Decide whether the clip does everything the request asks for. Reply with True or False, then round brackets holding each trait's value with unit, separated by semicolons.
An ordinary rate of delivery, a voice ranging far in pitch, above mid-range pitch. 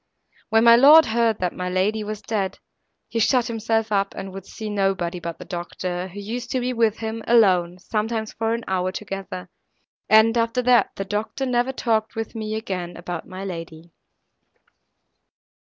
False (170 wpm; 3.7 semitones; 215 Hz)